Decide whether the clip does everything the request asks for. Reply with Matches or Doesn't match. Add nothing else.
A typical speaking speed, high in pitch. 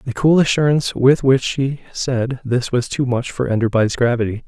Doesn't match